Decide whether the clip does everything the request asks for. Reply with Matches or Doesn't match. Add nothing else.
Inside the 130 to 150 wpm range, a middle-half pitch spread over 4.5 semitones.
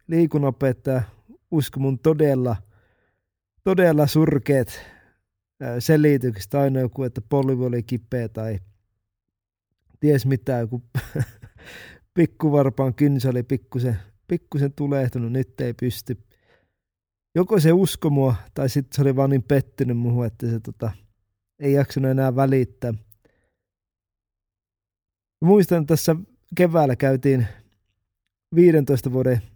Doesn't match